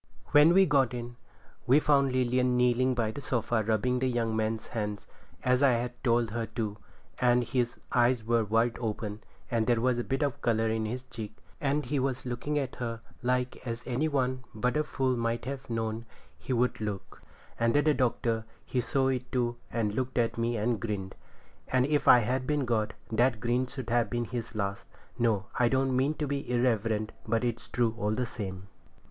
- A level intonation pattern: Yes, narrow, 2.3 semitones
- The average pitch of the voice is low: Yes, low, 120 Hz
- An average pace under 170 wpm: No, average, 195 wpm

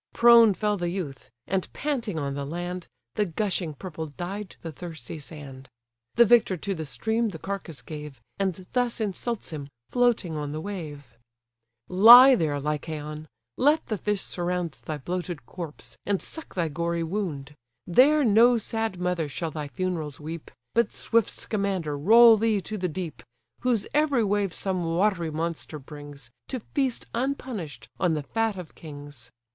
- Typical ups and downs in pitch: No, wide, 5.9 semitones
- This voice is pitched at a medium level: Yes, medium, 180 Hz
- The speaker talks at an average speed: Yes, average, 160 wpm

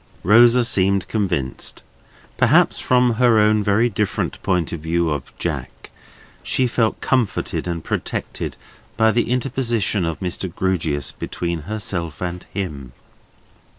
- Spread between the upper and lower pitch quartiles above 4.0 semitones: Yes, average, 5.0 semitones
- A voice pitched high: No, very low, 95 Hz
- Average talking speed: No, slow, 125 wpm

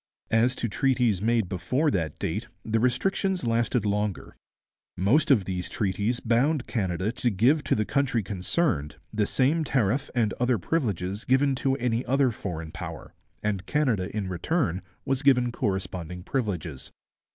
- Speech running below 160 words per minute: Yes, average, 150 wpm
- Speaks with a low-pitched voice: Yes, low, 115 Hz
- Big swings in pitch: Yes, wide, 5.7 semitones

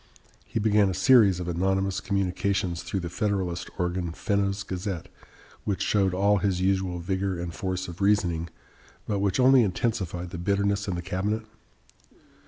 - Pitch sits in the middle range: No, very low, 95 Hz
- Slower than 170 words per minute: Yes, average, 155 wpm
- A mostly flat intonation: Yes, narrow, 2.2 semitones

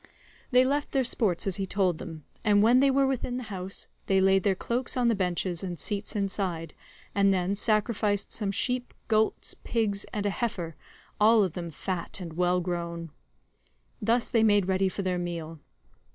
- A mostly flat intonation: No, average, 3.8 semitones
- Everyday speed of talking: Yes, average, 180 wpm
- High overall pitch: Yes, high, 200 Hz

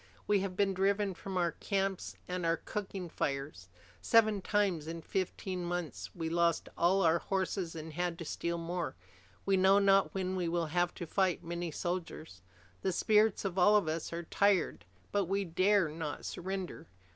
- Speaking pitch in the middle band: Yes, medium, 180 Hz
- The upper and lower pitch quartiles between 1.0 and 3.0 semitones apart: Yes, narrow, 2.6 semitones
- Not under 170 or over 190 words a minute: Yes, average, 175 wpm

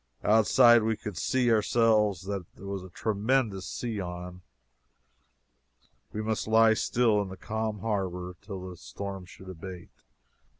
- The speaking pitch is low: Yes, low, 100 Hz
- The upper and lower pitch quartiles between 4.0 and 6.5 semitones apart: No, average, 3.1 semitones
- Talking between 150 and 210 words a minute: No, average, 140 wpm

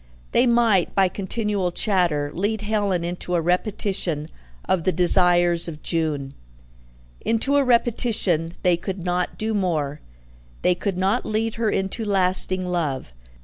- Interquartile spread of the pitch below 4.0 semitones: Yes, average, 3.6 semitones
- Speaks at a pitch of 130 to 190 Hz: Yes, medium, 185 Hz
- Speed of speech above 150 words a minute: No, average, 140 wpm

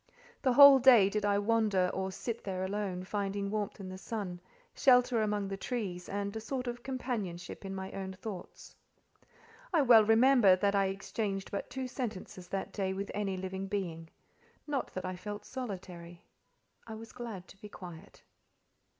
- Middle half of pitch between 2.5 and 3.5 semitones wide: Yes, average, 3.2 semitones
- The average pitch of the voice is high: Yes, high, 200 Hz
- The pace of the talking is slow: No, average, 170 wpm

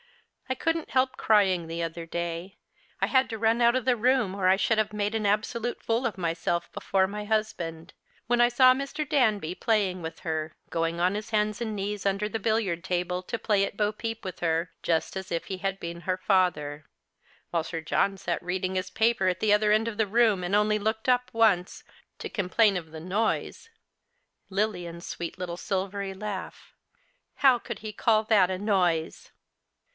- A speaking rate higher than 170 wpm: Yes, average, 200 wpm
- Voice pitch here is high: Yes, high, 200 Hz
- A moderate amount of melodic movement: Yes, average, 3.7 semitones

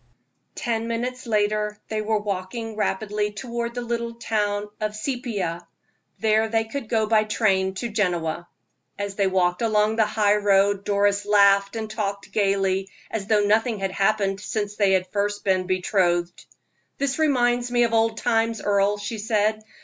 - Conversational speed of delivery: Yes, average, 155 wpm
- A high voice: Yes, high, 210 Hz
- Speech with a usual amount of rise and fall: No, narrow, 2.1 semitones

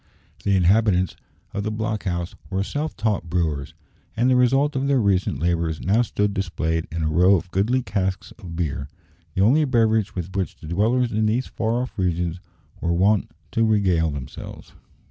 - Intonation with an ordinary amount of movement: Yes, average, 4.5 semitones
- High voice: No, very low, 95 Hz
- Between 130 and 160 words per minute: No, average, 180 wpm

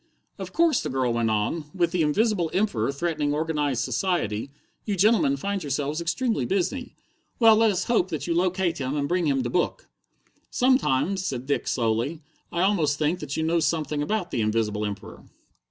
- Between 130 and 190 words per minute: Yes, average, 180 wpm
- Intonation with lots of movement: Yes, wide, 5.7 semitones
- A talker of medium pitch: Yes, medium, 160 Hz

